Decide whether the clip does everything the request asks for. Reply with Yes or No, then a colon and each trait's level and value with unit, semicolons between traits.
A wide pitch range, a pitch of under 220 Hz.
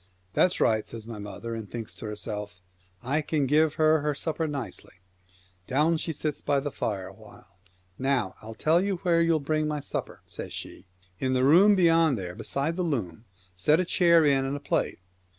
Yes: wide, 6.5 semitones; medium, 140 Hz